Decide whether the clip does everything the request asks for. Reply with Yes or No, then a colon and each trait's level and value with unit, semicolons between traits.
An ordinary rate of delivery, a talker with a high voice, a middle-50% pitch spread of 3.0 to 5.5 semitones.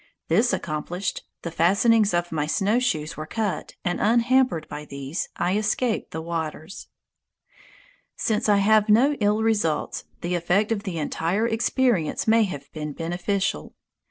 Yes: average, 145 wpm; high, 195 Hz; average, 5.2 semitones